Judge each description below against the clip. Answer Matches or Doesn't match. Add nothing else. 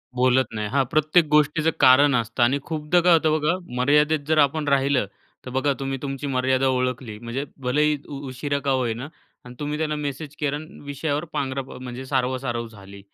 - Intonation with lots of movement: Doesn't match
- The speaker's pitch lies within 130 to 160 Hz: Matches